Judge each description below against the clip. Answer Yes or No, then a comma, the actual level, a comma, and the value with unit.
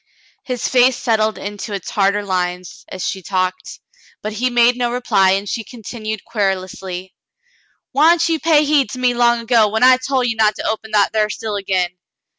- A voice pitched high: Yes, high, 220 Hz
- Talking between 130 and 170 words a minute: No, average, 185 wpm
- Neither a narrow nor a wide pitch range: Yes, average, 4.1 semitones